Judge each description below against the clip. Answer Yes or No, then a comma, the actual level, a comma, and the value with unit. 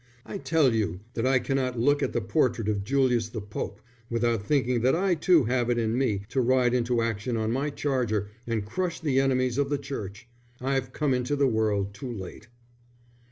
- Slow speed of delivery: No, average, 200 wpm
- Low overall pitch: Yes, low, 125 Hz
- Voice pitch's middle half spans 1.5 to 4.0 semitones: Yes, average, 3.5 semitones